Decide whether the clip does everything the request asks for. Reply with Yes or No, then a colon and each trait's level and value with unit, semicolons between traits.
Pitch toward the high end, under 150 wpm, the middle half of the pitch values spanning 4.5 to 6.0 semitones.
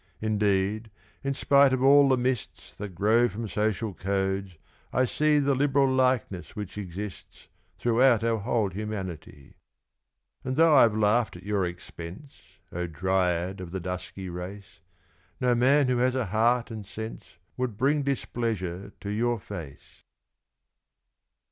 No: low, 110 Hz; average, 140 wpm; average, 5.1 semitones